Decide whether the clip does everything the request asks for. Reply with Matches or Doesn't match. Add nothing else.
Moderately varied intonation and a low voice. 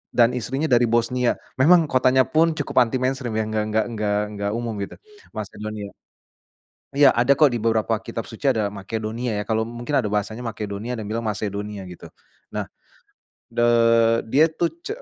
Matches